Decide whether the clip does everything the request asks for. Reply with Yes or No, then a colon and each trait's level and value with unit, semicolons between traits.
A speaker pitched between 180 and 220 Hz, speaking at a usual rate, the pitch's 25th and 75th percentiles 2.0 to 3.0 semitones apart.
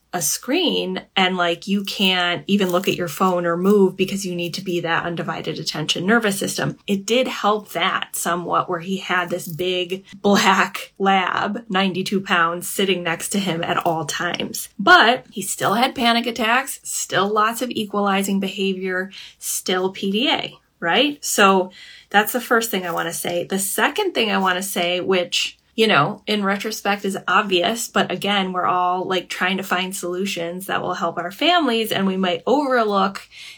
Yes: high, 190 Hz; average, 175 wpm; narrow, 2.5 semitones